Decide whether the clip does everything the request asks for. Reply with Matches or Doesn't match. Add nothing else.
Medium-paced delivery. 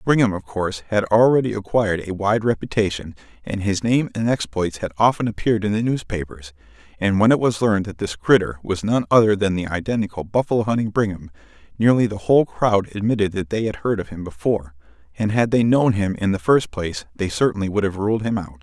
Doesn't match